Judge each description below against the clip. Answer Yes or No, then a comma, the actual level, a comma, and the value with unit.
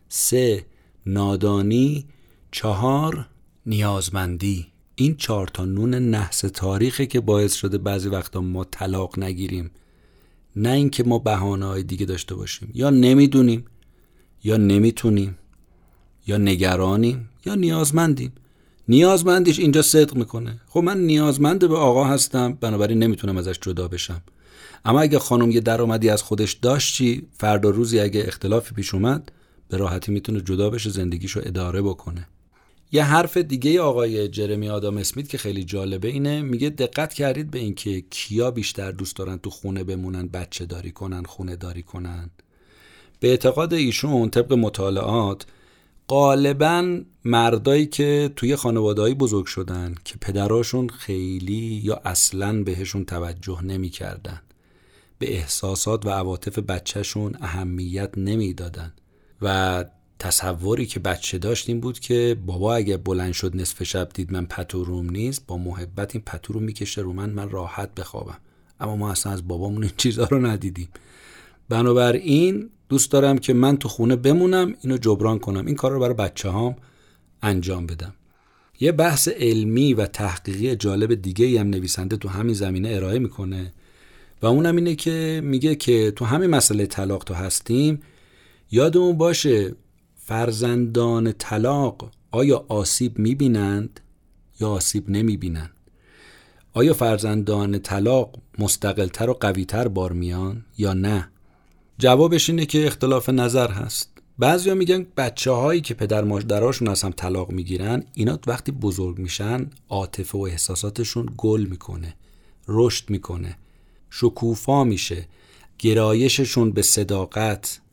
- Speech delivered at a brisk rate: No, average, 135 wpm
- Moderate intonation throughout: Yes, average, 4.8 semitones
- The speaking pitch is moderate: No, low, 105 Hz